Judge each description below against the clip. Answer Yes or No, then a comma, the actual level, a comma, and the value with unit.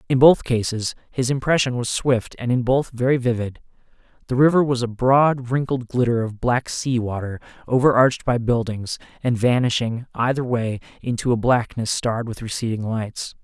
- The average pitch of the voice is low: Yes, low, 120 Hz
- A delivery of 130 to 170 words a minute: Yes, average, 165 wpm